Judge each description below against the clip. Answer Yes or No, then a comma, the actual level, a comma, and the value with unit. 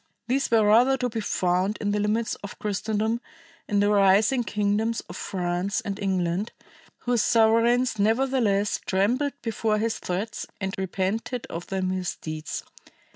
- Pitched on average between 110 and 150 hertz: No, high, 210 Hz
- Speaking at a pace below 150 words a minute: Yes, average, 140 wpm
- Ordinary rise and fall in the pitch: Yes, average, 3.0 semitones